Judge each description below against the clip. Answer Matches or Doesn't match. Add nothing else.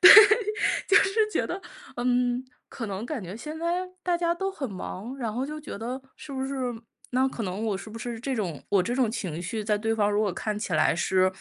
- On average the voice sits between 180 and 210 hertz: Doesn't match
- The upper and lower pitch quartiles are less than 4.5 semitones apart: Doesn't match